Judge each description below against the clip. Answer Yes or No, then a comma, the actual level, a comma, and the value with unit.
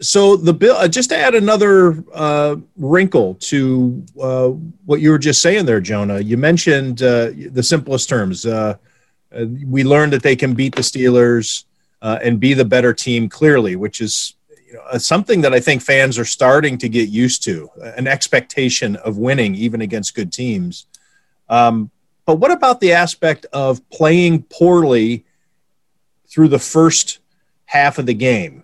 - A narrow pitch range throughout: No, average, 5.1 semitones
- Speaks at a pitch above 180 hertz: No, low, 135 Hz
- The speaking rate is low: No, average, 170 wpm